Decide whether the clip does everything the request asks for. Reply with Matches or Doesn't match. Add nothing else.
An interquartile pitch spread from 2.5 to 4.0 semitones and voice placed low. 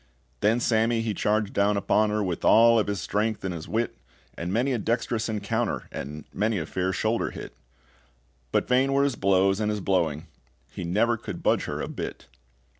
Matches